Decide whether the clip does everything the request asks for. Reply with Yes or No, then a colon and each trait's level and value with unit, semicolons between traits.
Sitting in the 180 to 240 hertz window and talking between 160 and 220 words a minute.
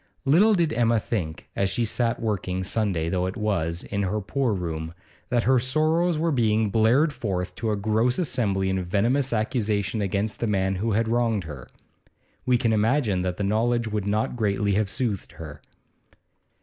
No: low, 110 Hz; average, 175 wpm